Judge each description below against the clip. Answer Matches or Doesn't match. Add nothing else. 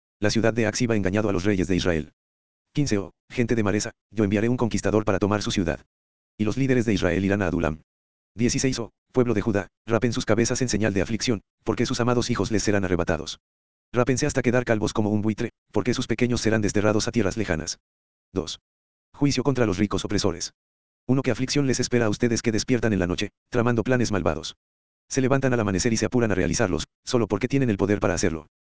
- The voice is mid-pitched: Doesn't match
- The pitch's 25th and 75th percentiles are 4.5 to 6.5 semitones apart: Matches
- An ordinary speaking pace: Doesn't match